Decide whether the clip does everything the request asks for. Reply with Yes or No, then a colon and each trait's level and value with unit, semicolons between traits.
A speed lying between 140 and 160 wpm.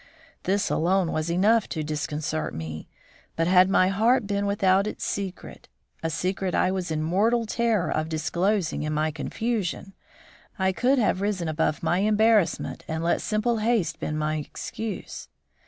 Yes: average, 155 wpm